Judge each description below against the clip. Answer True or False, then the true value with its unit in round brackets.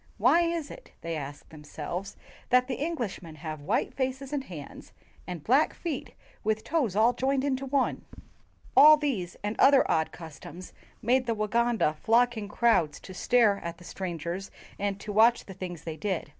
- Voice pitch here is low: False (215 Hz)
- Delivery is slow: False (170 wpm)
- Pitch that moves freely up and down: True (7.1 semitones)